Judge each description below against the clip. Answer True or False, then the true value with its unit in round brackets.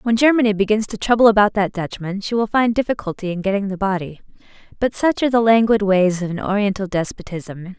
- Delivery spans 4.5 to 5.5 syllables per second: False (6.1 syllables/s)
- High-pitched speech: True (205 Hz)